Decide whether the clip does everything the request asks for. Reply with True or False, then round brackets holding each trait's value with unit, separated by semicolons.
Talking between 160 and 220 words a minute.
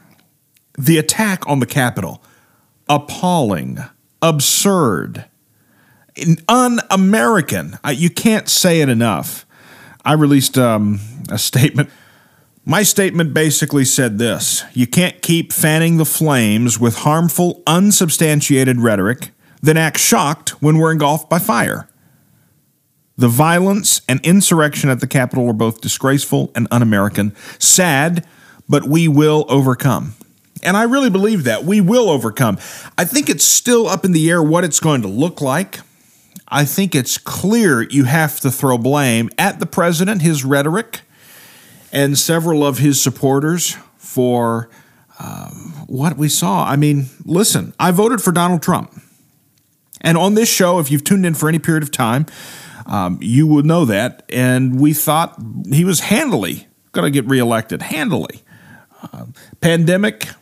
False (145 wpm)